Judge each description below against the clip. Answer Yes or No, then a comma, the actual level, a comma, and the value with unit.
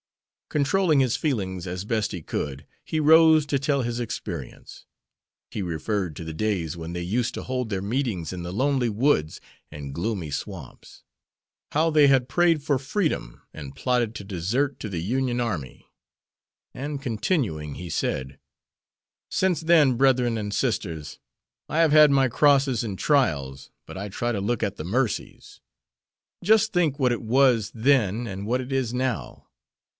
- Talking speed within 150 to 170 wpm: Yes, average, 160 wpm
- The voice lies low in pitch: Yes, low, 120 Hz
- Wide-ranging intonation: Yes, wide, 6.8 semitones